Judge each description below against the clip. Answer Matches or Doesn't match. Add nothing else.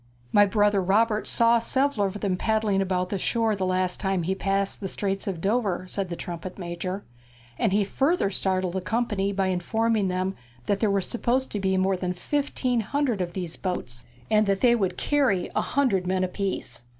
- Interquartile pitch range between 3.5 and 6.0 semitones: Doesn't match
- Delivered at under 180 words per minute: Doesn't match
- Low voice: Doesn't match